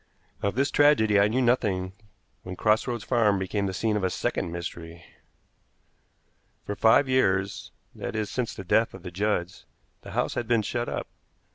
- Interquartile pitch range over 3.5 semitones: Yes, average, 3.9 semitones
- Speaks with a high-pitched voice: No, low, 105 Hz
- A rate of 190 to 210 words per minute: No, average, 175 wpm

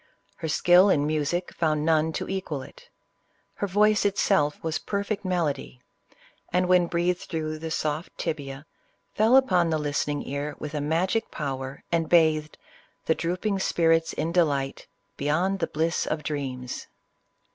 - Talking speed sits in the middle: Yes, average, 150 wpm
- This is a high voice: No, medium, 160 Hz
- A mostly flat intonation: No, average, 3.4 semitones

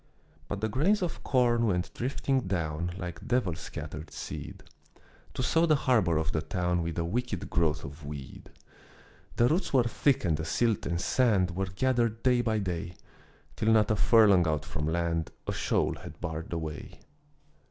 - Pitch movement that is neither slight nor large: No, wide, 6.5 semitones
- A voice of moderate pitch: No, very low, 95 Hz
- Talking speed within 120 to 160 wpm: No, average, 175 wpm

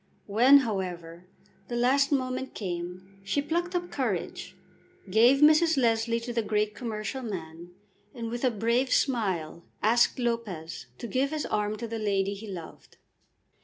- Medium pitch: No, high, 225 Hz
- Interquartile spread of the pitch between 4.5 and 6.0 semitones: Yes, average, 4.8 semitones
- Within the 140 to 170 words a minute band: Yes, average, 150 wpm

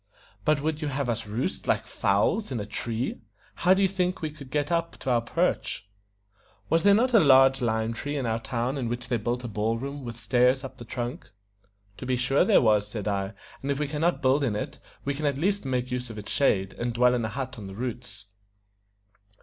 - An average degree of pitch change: Yes, average, 3.9 semitones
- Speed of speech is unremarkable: No, fast, 235 wpm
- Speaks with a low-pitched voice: Yes, low, 125 Hz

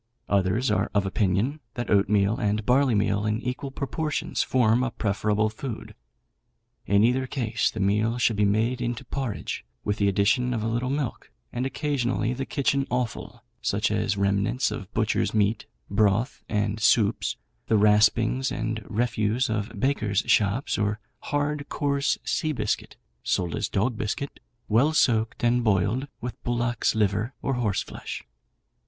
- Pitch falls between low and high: No, low, 115 Hz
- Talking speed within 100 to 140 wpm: No, average, 150 wpm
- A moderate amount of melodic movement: Yes, average, 3.5 semitones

